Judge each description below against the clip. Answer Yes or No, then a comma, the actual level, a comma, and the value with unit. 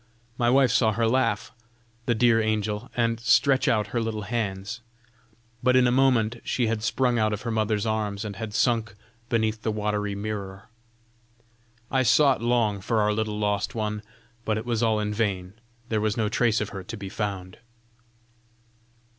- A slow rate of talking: No, average, 175 wpm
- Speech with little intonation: Yes, narrow, 2.0 semitones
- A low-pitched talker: Yes, low, 110 Hz